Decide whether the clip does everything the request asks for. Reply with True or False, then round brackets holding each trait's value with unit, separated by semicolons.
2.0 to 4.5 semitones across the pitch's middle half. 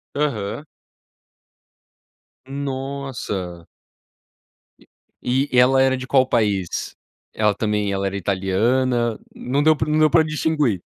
False (5.4 semitones)